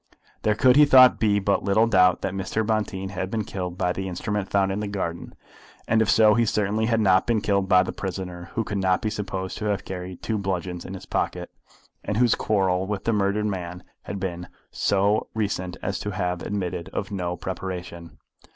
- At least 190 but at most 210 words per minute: Yes, fast, 205 wpm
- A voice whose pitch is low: Yes, very low, 95 Hz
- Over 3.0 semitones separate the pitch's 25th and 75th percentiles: No, narrow, 2.4 semitones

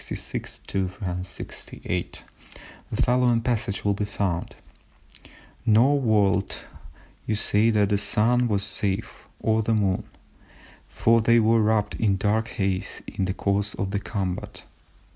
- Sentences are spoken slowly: Yes, slow, 130 wpm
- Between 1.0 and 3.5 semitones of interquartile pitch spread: Yes, narrow, 2.4 semitones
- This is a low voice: Yes, low, 105 Hz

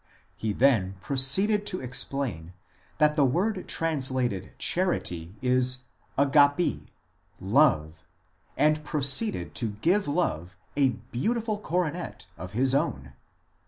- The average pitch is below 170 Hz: Yes, low, 135 Hz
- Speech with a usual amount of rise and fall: No, wide, 7.5 semitones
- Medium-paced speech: No, slow, 110 wpm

